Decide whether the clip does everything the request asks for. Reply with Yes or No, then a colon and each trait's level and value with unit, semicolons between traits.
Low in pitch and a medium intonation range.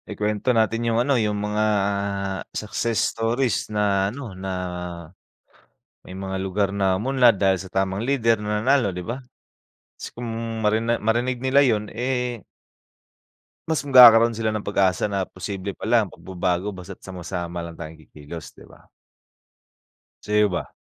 Yes: low, 105 Hz; average, 3.6 semitones